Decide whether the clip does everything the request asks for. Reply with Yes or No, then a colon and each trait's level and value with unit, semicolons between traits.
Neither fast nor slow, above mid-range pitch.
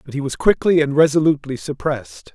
No: average, 180 wpm; medium, 145 Hz